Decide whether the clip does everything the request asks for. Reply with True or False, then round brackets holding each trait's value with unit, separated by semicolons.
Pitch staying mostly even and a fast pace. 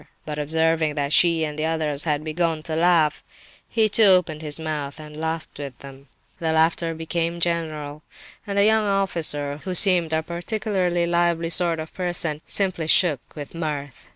False (2.3 semitones; 170 wpm)